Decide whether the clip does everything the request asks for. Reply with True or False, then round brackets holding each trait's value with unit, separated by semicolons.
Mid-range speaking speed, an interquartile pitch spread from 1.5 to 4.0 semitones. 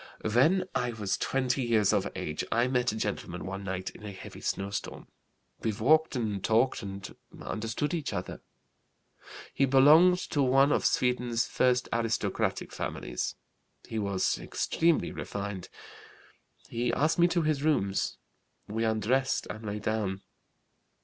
False (145 wpm; 4.8 semitones)